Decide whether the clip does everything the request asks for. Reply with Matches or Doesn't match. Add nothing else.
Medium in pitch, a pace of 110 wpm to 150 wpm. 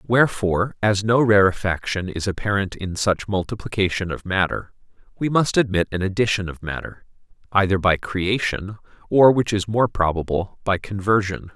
Doesn't match